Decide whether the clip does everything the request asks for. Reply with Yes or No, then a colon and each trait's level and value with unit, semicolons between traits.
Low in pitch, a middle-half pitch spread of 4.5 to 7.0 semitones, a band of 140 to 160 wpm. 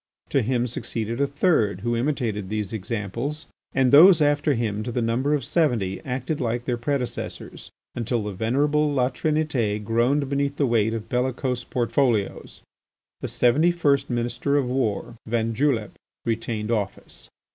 No: low, 120 Hz; average, 3.8 semitones; average, 150 wpm